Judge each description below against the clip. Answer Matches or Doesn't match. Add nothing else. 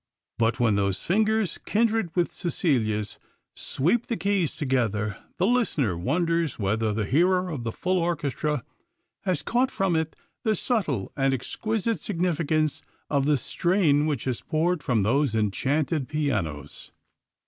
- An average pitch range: Doesn't match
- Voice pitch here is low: Doesn't match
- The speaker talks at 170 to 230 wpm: Doesn't match